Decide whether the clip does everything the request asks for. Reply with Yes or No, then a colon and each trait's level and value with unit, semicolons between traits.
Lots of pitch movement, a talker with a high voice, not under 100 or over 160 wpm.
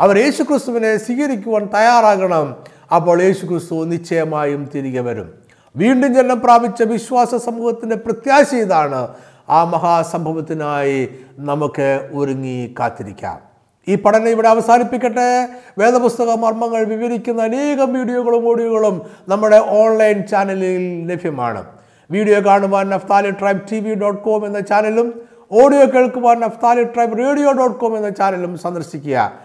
Yes: wide, 6.3 semitones; high, 210 Hz; average, 115 wpm